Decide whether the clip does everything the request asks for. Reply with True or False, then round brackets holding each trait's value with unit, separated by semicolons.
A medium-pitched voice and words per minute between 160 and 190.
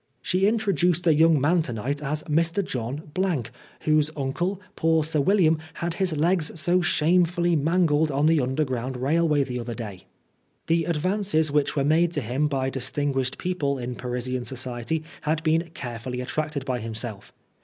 True (150 Hz; 165 wpm)